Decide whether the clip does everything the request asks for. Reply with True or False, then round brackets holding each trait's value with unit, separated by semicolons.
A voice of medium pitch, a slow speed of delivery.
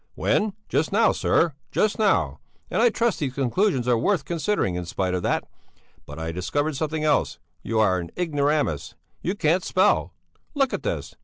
False (150 Hz; 175 wpm)